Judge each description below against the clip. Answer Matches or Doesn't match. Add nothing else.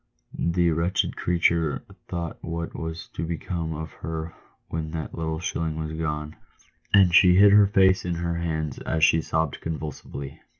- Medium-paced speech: Matches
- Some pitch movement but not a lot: Doesn't match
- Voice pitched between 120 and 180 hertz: Doesn't match